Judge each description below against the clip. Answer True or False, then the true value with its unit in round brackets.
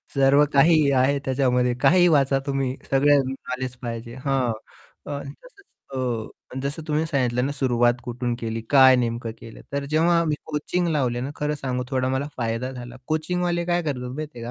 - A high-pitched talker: False (135 Hz)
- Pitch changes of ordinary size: True (3.0 semitones)